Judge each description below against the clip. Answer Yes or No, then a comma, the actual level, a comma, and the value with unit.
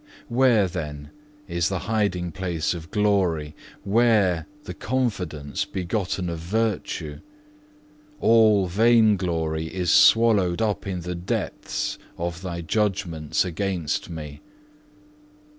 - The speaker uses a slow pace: Yes, slow, 110 wpm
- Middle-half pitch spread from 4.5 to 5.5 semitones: No, average, 4.1 semitones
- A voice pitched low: Yes, very low, 90 Hz